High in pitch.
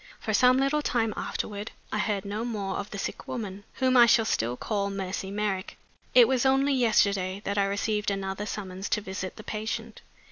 Yes: high, 210 Hz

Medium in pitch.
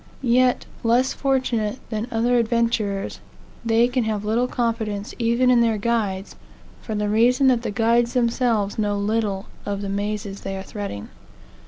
No: high, 225 Hz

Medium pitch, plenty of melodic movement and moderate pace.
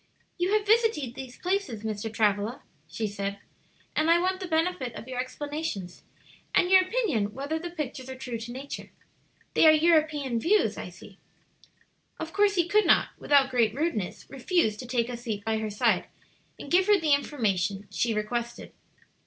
No: very high, 265 Hz; wide, 7.3 semitones; average, 175 wpm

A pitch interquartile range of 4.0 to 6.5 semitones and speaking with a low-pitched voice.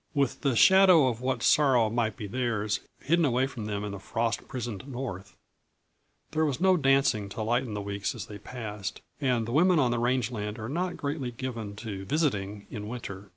Yes: average, 4.6 semitones; low, 120 Hz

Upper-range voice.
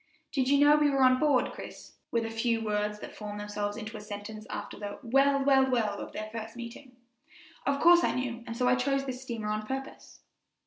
Yes: high, 235 Hz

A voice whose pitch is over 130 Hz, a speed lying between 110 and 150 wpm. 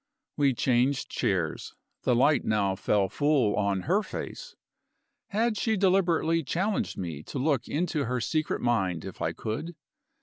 Yes: medium, 140 Hz; average, 145 wpm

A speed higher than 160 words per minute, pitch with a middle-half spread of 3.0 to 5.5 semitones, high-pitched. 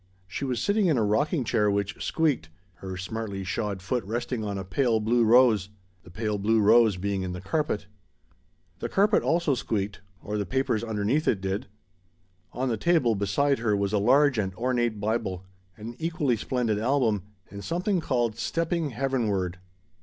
No: average, 170 wpm; average, 4.6 semitones; low, 110 Hz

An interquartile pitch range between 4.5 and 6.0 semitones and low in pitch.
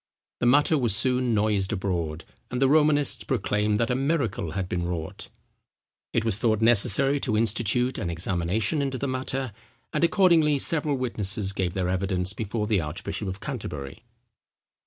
Yes: wide, 5.6 semitones; low, 110 Hz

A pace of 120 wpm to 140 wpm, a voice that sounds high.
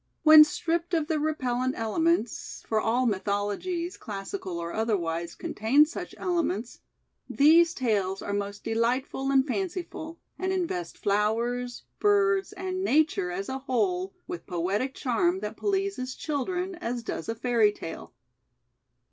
Yes: slow, 135 wpm; very high, 255 Hz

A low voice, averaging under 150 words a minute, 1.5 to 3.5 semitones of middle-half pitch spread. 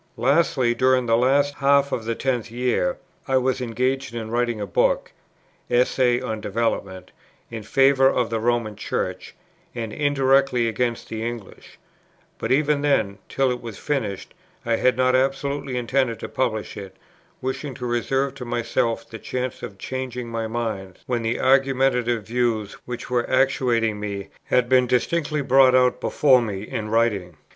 No: low, 125 Hz; average, 160 wpm; average, 2.7 semitones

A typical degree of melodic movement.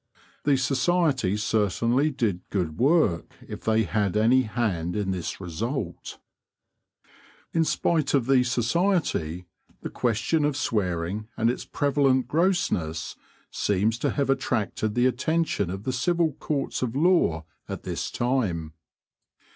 No: wide, 6.3 semitones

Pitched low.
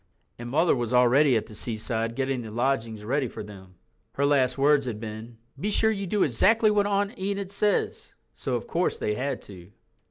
Yes: low, 130 Hz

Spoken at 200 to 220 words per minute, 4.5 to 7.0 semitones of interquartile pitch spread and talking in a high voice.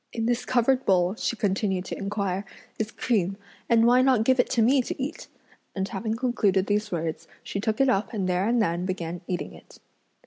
No: fast, 205 wpm; average, 4.1 semitones; high, 210 Hz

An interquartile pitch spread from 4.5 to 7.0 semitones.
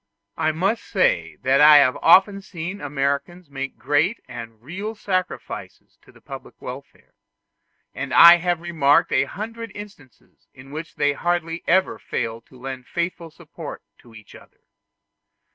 Yes: average, 5.0 semitones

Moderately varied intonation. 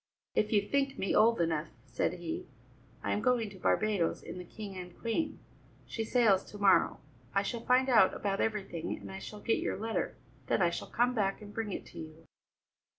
Yes: average, 3.7 semitones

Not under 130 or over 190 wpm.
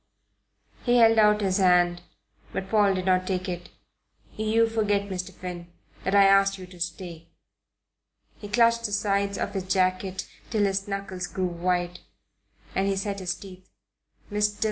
Yes: average, 160 wpm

